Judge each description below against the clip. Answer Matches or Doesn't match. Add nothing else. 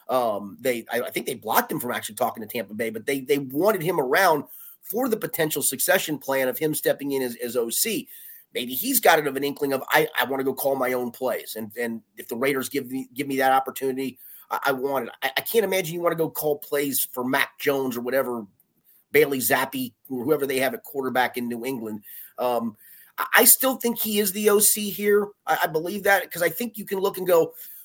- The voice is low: Doesn't match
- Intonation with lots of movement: Matches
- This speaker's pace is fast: Matches